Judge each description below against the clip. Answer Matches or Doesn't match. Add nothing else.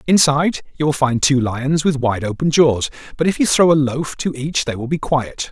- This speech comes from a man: Matches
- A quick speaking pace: Matches